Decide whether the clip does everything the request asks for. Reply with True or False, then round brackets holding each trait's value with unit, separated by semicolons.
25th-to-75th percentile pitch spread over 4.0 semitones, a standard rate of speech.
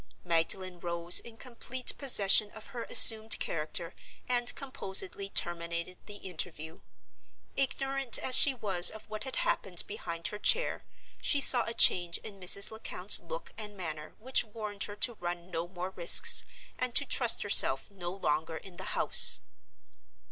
True (5.1 semitones; 155 wpm)